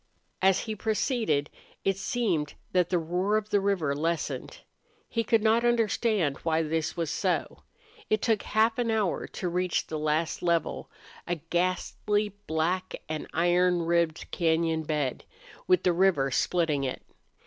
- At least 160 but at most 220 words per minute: No, average, 150 wpm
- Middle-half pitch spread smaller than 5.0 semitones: Yes, average, 4.6 semitones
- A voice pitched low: No, medium, 175 Hz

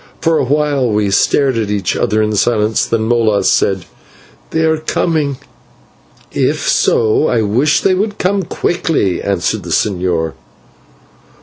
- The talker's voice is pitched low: Yes, low, 115 Hz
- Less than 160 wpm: Yes, average, 140 wpm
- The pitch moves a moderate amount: No, wide, 6.9 semitones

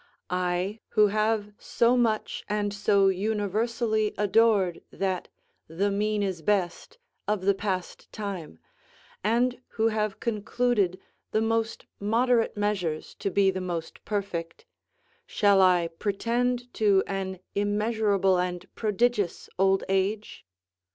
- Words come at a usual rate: No, slow, 115 wpm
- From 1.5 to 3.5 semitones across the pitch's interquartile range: Yes, narrow, 2.5 semitones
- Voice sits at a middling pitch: No, high, 205 Hz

